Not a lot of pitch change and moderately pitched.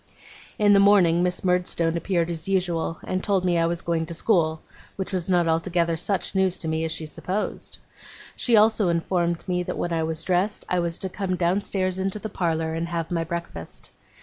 Yes: narrow, 2.3 semitones; medium, 175 Hz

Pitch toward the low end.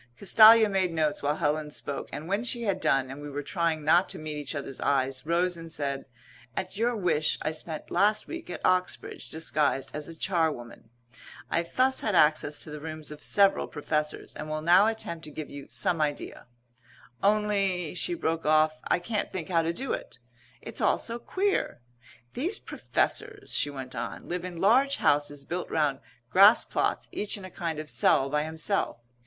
No: medium, 165 Hz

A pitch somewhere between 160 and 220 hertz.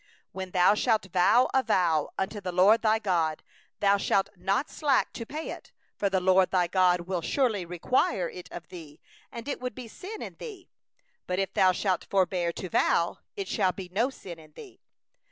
Yes: high, 190 Hz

